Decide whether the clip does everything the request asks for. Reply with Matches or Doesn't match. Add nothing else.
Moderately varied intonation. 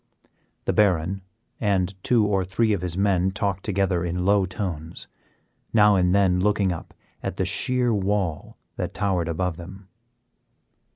Doesn't match